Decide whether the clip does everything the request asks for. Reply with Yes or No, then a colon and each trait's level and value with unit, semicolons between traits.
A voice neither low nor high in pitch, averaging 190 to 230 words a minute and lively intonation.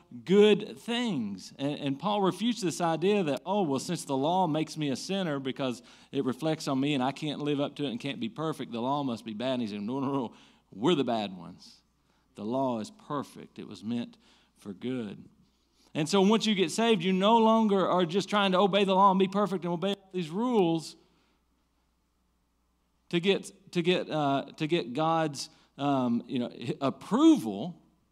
Yes: medium, 160 Hz; fast, 205 wpm; wide, 6.7 semitones